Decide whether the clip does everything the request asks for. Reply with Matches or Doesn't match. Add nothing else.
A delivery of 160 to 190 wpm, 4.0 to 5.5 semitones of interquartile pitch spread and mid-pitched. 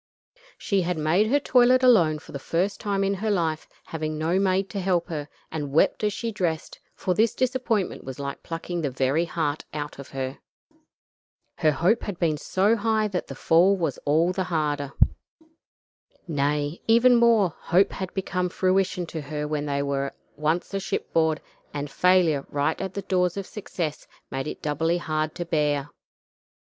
Matches